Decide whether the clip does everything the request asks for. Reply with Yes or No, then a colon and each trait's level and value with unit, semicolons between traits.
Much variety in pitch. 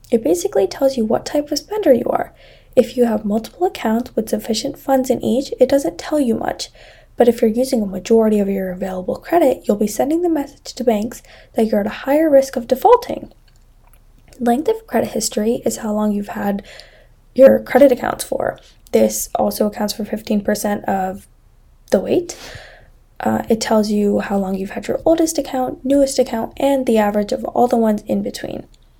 No: average, 4.3 semitones